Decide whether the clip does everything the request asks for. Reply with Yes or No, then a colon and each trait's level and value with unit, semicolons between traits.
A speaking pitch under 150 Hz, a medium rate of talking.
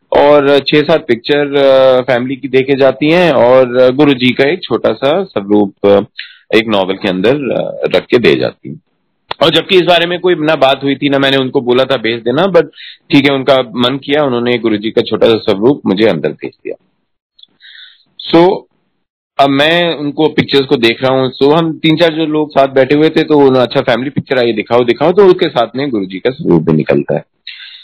No: medium, 140 Hz; fast, 215 wpm